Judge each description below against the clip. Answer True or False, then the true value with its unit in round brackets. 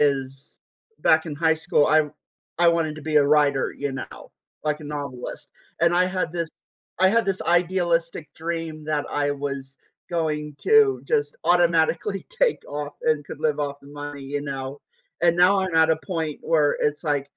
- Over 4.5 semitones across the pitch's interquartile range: False (2.9 semitones)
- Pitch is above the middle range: False (155 Hz)